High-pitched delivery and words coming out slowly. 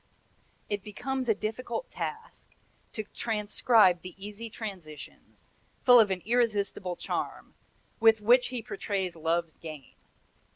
Yes: high, 210 Hz; slow, 120 wpm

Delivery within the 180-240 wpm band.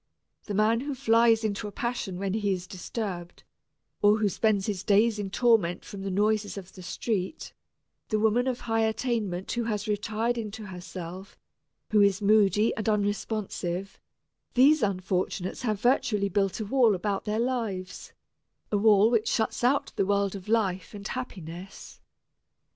No: average, 160 wpm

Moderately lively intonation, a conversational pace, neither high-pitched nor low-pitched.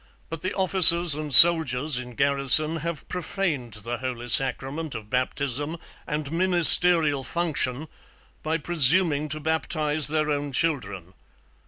No: average, 3.8 semitones; slow, 125 wpm; medium, 150 Hz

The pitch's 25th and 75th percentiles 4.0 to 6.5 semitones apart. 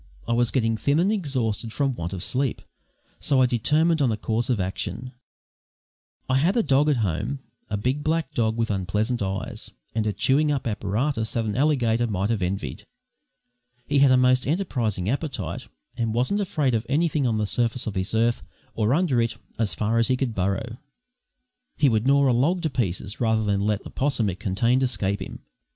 Yes: average, 4.5 semitones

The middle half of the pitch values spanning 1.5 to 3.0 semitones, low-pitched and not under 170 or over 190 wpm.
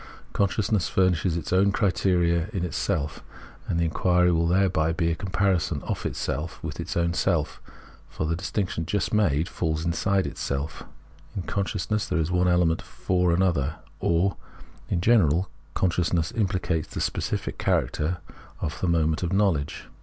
No: narrow, 2.6 semitones; very low, 90 Hz; average, 160 wpm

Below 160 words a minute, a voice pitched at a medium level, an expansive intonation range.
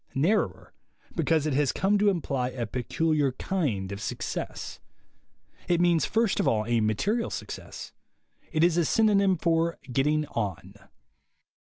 Yes: average, 140 wpm; medium, 155 Hz; wide, 6.0 semitones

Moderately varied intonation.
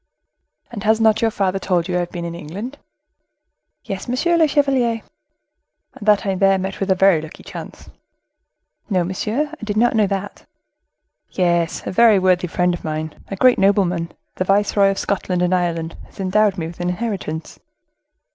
Yes: average, 3.4 semitones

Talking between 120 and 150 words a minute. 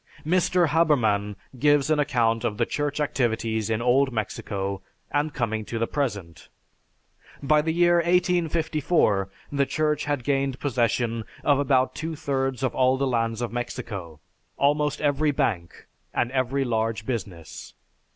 Yes: average, 140 wpm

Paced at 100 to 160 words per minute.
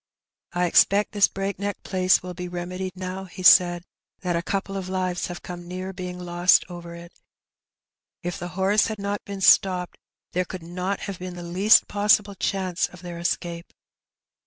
No: average, 180 wpm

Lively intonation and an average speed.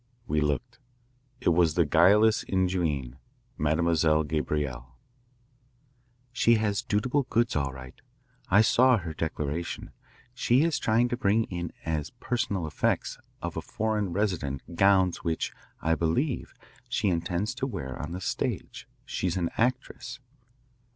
No: wide, 6.2 semitones; slow, 130 wpm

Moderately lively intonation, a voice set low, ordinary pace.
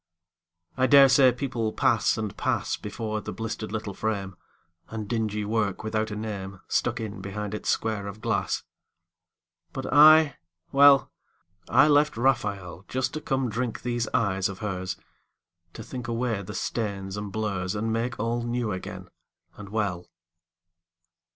Yes: average, 3.3 semitones; low, 110 Hz; average, 150 wpm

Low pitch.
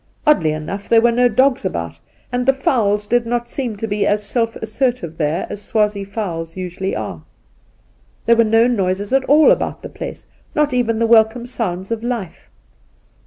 No: high, 220 Hz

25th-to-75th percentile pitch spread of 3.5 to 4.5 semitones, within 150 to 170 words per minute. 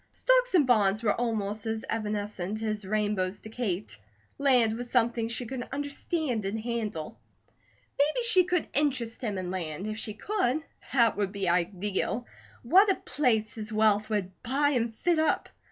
Yes: average, 4.2 semitones; average, 165 wpm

